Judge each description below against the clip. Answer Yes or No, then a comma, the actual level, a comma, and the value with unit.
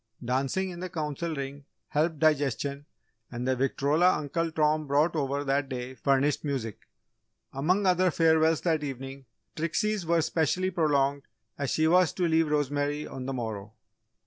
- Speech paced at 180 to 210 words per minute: No, average, 150 wpm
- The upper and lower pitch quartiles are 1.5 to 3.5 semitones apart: Yes, average, 3.2 semitones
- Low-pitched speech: No, medium, 145 Hz